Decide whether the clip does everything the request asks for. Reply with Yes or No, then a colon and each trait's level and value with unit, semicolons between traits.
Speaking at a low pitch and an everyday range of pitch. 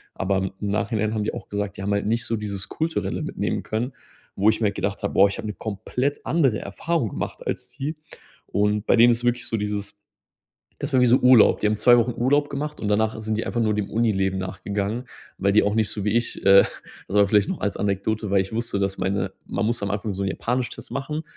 Yes: low, 105 Hz; average, 3.0 semitones